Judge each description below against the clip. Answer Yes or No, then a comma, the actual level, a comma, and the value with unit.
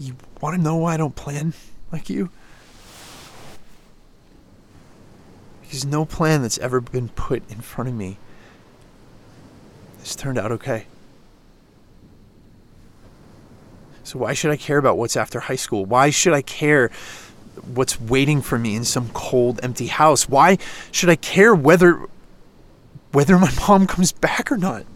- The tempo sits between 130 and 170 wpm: Yes, average, 145 wpm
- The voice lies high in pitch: No, low, 130 Hz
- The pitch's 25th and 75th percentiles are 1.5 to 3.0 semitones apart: No, average, 4.8 semitones